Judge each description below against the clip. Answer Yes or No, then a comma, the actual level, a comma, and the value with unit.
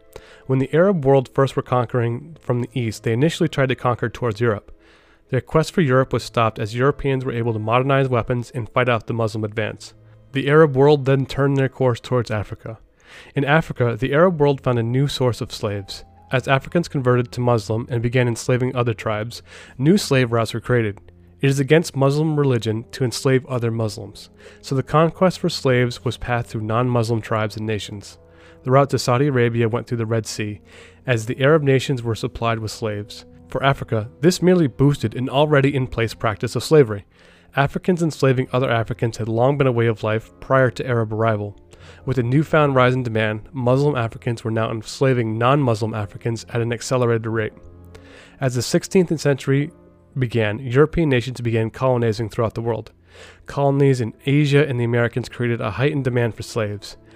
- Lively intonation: No, average, 3.4 semitones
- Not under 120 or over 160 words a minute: No, average, 185 wpm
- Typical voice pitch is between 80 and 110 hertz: No, low, 125 Hz